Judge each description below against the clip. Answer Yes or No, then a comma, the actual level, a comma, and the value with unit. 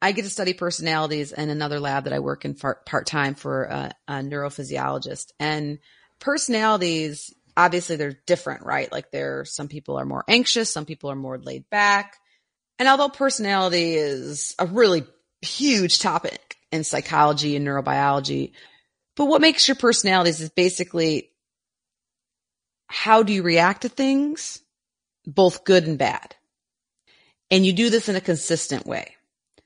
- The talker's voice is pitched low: No, medium, 170 Hz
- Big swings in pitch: Yes, wide, 5.9 semitones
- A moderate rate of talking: Yes, average, 150 wpm